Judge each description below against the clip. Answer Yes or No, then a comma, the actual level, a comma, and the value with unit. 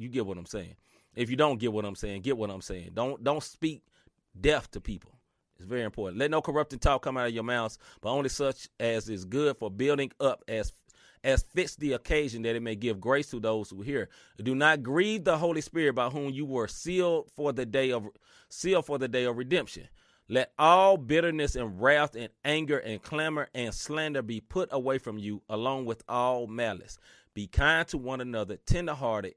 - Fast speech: Yes, fast, 210 wpm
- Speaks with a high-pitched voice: No, low, 130 Hz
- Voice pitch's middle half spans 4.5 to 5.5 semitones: Yes, average, 4.9 semitones